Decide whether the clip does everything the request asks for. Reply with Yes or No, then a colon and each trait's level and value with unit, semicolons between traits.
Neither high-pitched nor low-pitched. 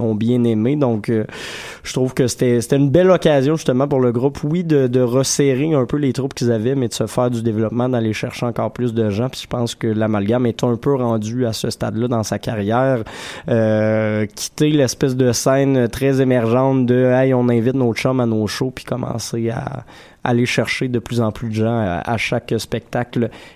No: low, 125 Hz